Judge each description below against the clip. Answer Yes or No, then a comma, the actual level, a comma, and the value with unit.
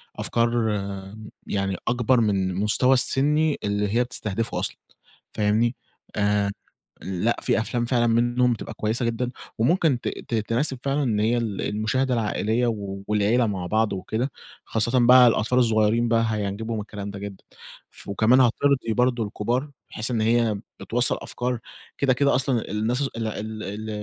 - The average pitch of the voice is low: Yes, low, 115 Hz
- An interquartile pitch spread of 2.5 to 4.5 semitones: Yes, average, 2.8 semitones